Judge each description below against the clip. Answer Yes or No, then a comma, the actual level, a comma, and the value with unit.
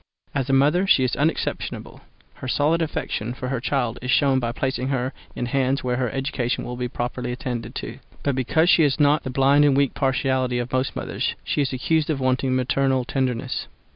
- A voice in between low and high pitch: No, low, 130 Hz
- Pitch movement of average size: No, narrow, 1.9 semitones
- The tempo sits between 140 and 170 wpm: No, average, 200 wpm